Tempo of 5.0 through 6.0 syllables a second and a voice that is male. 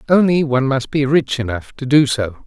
Yes: 5.2 syllables/s; male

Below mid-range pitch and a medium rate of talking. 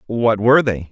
Yes: low, 110 Hz; average, 195 wpm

